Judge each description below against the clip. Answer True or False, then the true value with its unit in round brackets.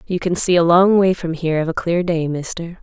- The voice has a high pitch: False (170 Hz)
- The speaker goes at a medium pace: False (275 wpm)